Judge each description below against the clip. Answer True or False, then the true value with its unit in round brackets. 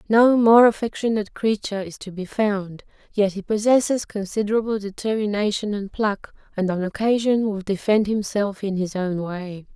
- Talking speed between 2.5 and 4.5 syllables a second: False (5.0 syllables/s)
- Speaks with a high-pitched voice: True (205 Hz)